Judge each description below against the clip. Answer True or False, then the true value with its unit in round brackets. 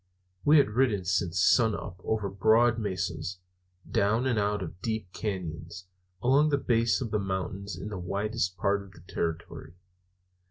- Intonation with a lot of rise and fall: False (3.3 semitones)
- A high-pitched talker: False (100 Hz)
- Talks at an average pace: True (155 wpm)